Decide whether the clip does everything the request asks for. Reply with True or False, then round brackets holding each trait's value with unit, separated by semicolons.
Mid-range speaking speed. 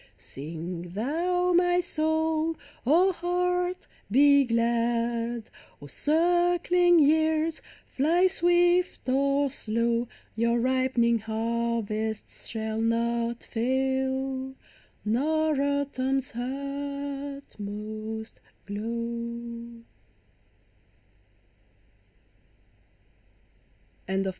False (60 wpm)